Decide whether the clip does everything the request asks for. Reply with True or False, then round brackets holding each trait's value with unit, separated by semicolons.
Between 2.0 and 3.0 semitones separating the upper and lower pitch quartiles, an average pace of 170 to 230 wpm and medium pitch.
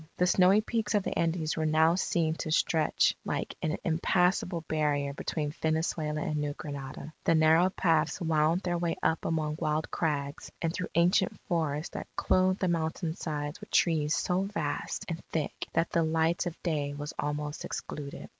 True (2.4 semitones; 175 wpm; 160 Hz)